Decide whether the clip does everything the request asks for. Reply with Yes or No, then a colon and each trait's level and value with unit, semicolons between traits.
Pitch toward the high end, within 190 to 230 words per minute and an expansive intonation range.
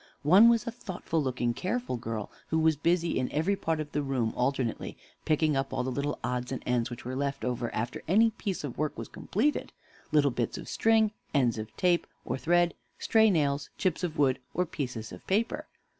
No: medium, 145 Hz; average, 200 wpm; wide, 6.1 semitones